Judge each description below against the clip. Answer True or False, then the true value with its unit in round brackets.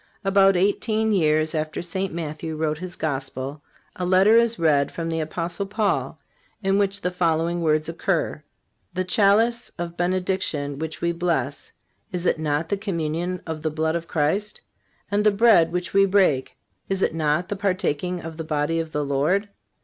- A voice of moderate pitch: True (170 Hz)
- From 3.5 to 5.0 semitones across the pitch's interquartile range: True (3.8 semitones)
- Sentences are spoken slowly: False (170 wpm)